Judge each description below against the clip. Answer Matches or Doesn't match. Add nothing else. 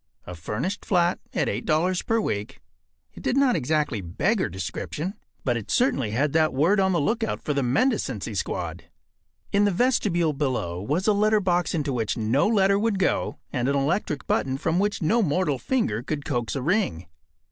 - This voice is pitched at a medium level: Matches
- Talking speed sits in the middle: Matches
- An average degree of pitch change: Doesn't match